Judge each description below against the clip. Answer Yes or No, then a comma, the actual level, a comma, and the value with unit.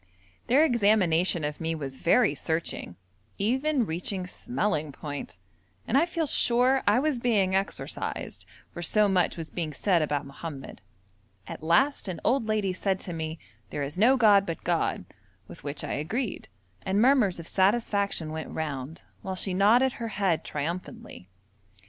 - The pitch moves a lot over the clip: Yes, wide, 6.2 semitones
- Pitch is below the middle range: No, high, 190 Hz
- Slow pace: No, average, 155 wpm